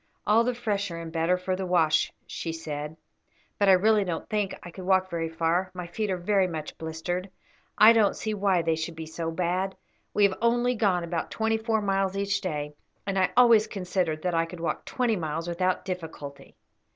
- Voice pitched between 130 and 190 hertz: Yes, medium, 185 Hz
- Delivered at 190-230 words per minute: Yes, average, 200 wpm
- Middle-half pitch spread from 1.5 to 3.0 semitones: No, average, 3.5 semitones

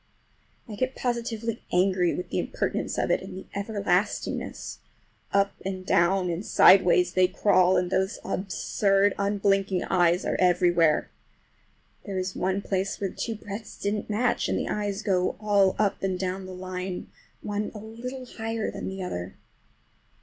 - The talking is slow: No, average, 155 wpm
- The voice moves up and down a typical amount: No, narrow, 2.1 semitones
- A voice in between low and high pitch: No, high, 195 Hz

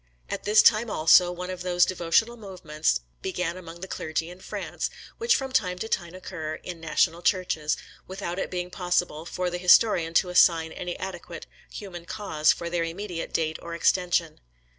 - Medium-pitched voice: Yes, medium, 175 Hz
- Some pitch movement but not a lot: No, narrow, 2.0 semitones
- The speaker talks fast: No, average, 175 wpm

